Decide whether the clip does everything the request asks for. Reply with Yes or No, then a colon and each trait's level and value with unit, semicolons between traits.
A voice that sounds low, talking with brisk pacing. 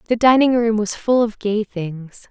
No: high, 215 Hz; fast, 210 wpm